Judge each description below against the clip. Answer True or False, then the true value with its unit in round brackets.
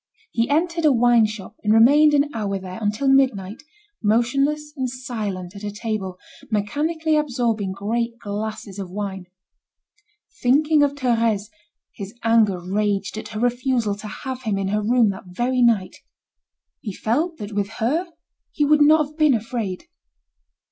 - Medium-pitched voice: False (230 Hz)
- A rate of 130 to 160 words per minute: True (155 wpm)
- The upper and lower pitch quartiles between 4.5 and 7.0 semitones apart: True (4.8 semitones)